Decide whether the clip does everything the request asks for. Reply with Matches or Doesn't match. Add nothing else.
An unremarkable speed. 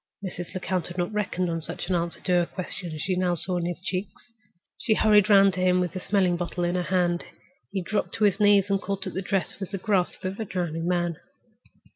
Doesn't match